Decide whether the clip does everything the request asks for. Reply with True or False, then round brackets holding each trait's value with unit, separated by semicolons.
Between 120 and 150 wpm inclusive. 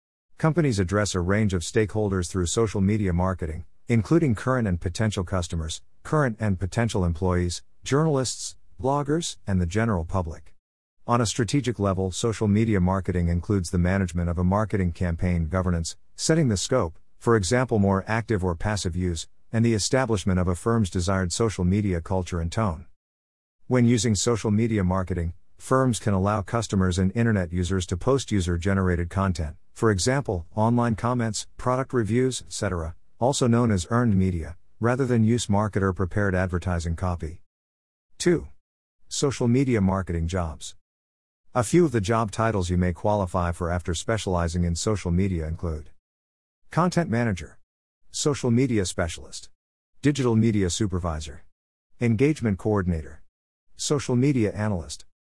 True (145 wpm)